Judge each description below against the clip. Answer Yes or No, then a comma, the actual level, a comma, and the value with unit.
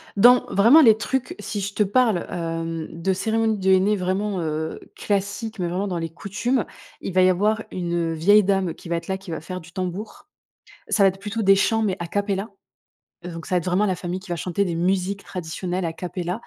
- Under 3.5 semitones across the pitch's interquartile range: Yes, average, 2.9 semitones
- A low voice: No, high, 190 Hz